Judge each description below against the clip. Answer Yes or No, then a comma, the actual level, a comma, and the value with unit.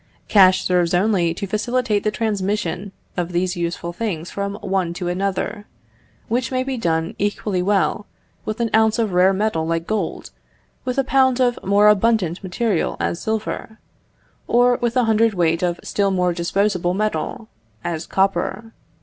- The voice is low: No, high, 200 Hz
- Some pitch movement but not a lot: Yes, average, 3.7 semitones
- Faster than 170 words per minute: No, average, 160 wpm